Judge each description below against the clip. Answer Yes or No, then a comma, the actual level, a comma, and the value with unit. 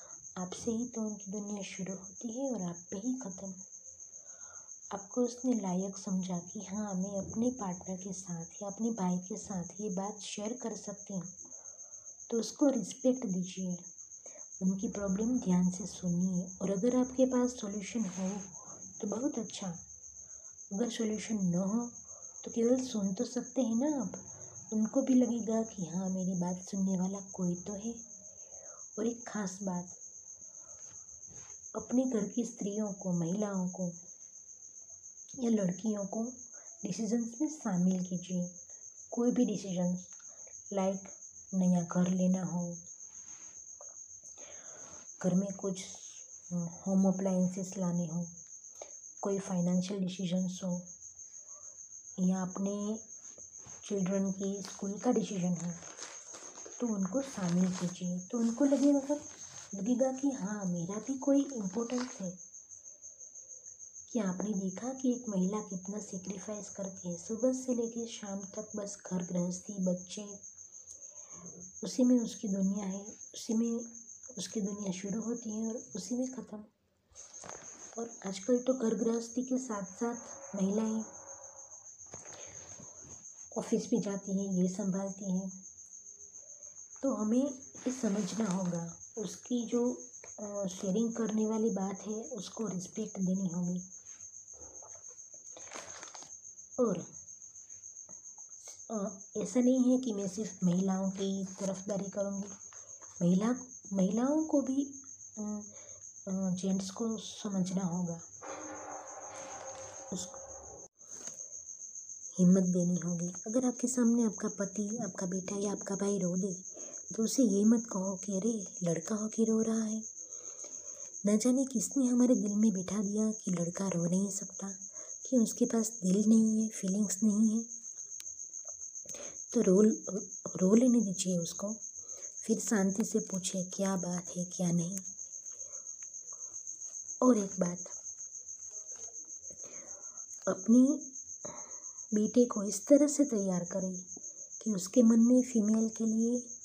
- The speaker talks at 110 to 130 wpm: Yes, average, 125 wpm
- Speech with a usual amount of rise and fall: Yes, average, 3.7 semitones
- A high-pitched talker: Yes, high, 205 Hz